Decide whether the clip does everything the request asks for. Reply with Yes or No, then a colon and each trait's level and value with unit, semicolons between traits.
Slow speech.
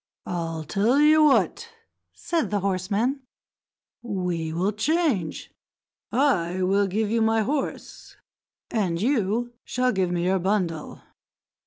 Yes: slow, 120 wpm